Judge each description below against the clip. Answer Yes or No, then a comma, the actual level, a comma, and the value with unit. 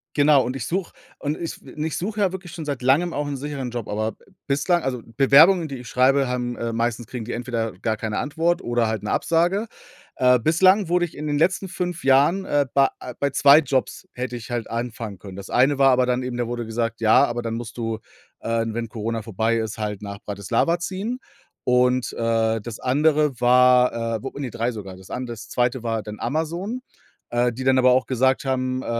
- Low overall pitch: Yes, low, 125 Hz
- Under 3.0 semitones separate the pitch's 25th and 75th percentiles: No, average, 4.2 semitones